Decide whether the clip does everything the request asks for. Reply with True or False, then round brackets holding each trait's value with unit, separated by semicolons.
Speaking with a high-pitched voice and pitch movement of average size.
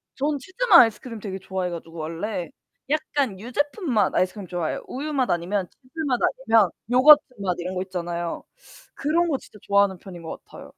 False (210 Hz; 7.4 semitones)